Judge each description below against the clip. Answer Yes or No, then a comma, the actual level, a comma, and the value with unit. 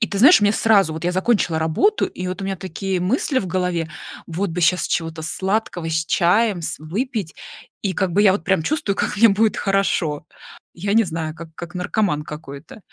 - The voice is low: No, medium, 185 Hz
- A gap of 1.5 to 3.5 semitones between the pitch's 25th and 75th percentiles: No, average, 4.0 semitones